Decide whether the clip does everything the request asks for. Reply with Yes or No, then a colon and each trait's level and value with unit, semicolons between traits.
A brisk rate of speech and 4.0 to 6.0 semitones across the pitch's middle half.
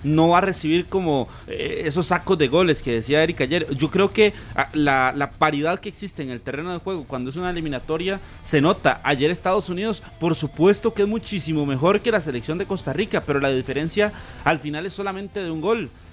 Yes: fast, 210 wpm; average, 5.3 semitones